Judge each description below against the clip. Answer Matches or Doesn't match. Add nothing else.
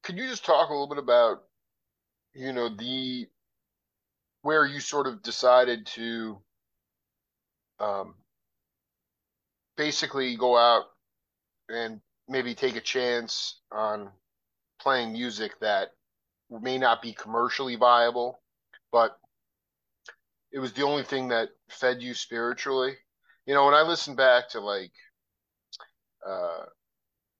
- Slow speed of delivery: Matches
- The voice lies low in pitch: Matches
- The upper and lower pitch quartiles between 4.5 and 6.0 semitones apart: Doesn't match